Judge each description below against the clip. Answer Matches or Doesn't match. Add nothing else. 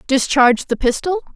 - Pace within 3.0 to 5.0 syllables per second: Doesn't match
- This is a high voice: Matches